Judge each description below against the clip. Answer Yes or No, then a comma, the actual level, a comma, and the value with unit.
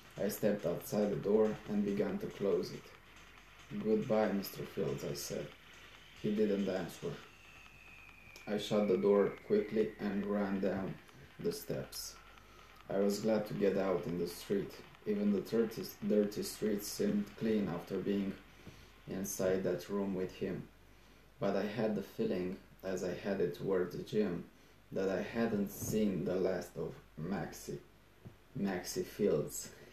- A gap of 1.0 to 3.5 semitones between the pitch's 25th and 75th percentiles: Yes, narrow, 2.6 semitones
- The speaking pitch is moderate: No, low, 100 Hz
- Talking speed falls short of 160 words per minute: Yes, average, 140 wpm